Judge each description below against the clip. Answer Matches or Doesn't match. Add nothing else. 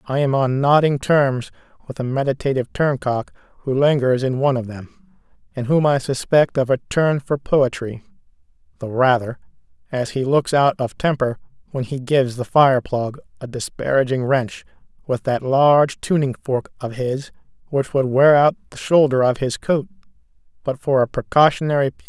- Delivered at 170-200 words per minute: Matches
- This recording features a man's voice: Matches